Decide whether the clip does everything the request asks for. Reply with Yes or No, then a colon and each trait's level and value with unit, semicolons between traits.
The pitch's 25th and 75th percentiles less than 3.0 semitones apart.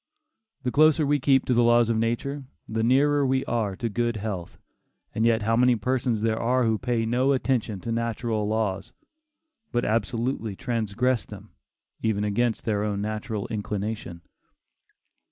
Yes: narrow, 2.6 semitones